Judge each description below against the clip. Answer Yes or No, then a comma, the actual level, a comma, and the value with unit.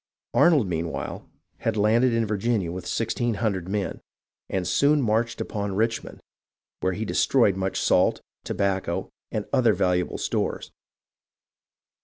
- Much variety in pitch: No, average, 3.5 semitones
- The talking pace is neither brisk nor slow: No, slow, 125 wpm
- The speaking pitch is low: Yes, low, 105 Hz